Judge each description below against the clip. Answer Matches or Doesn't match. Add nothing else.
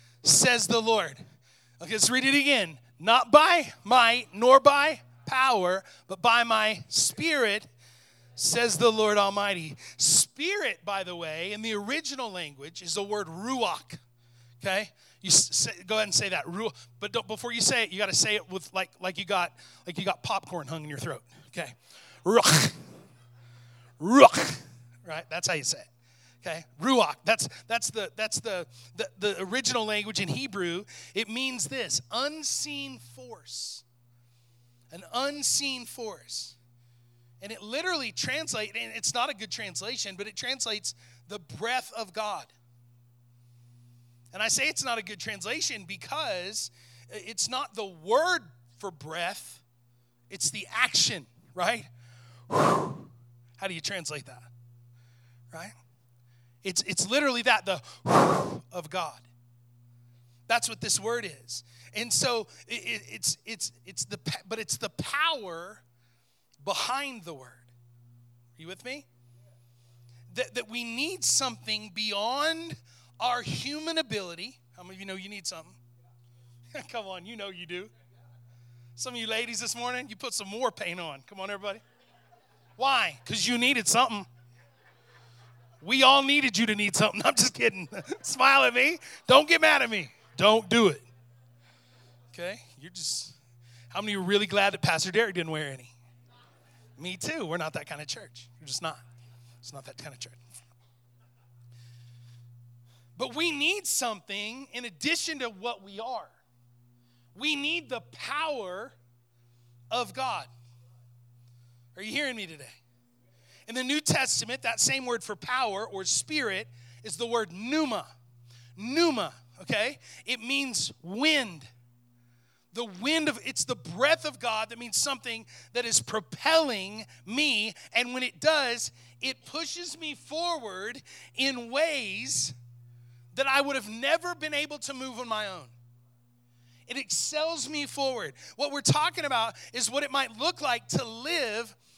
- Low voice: Doesn't match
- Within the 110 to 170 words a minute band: Matches